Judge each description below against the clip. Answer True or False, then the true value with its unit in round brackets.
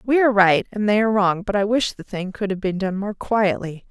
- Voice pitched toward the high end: True (200 Hz)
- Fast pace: True (275 wpm)